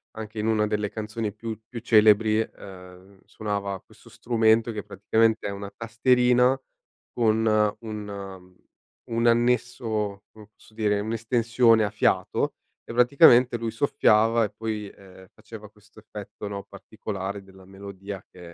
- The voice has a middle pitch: No, low, 110 Hz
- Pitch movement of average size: No, narrow, 2.3 semitones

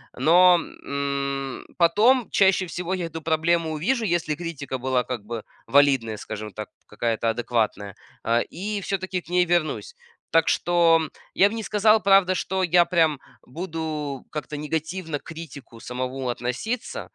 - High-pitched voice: No, medium, 160 Hz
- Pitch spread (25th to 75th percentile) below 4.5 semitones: No, wide, 5.4 semitones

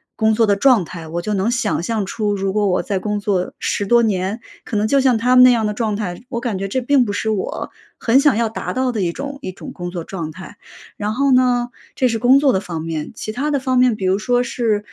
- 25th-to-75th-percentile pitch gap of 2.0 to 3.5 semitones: No, average, 4.2 semitones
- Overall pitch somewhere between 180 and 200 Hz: No, high, 215 Hz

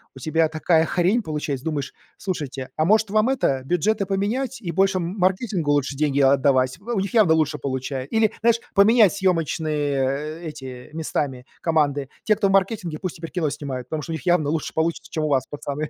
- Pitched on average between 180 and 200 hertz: No, medium, 160 Hz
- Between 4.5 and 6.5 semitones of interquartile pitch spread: Yes, average, 5.2 semitones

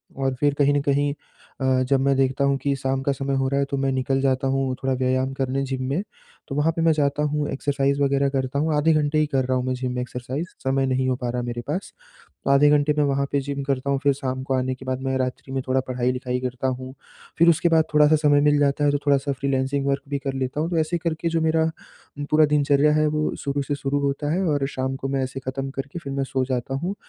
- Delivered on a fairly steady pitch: Yes, narrow, 1.8 semitones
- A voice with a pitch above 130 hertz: Yes, medium, 140 Hz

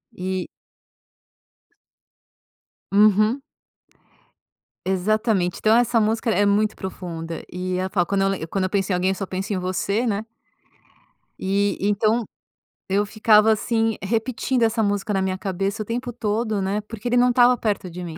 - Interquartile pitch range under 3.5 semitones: Yes, average, 2.8 semitones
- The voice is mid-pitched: No, high, 205 Hz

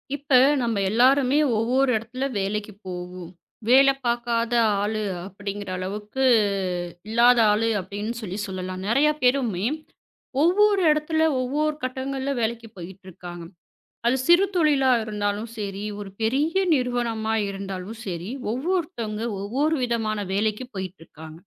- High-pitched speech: Yes, high, 225 Hz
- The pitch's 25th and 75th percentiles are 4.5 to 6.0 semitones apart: Yes, average, 4.9 semitones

